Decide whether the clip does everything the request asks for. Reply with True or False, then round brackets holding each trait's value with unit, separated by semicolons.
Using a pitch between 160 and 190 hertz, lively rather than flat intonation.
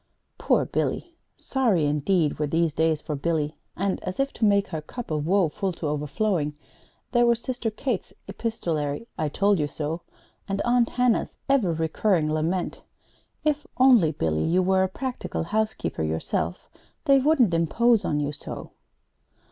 True (185 Hz; 7.0 semitones)